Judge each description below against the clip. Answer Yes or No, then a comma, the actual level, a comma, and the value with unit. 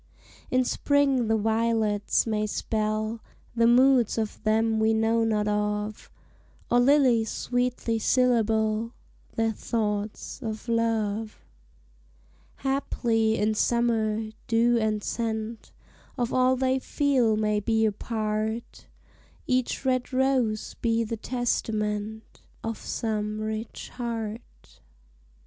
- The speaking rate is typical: No, slow, 110 wpm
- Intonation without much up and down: Yes, narrow, 1.9 semitones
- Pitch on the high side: Yes, high, 225 Hz